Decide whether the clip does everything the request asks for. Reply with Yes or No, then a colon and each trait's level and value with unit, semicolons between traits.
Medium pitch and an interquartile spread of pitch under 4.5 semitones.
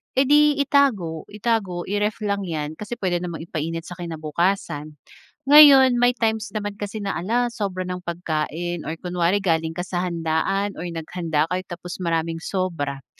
Yes: medium, 180 Hz; average, 4.0 semitones